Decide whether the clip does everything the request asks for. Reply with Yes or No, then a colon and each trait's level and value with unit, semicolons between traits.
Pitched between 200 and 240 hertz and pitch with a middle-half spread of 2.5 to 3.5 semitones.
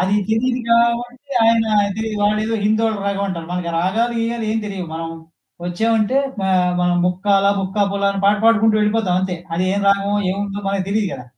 Yes: high, 205 Hz; average, 2.8 semitones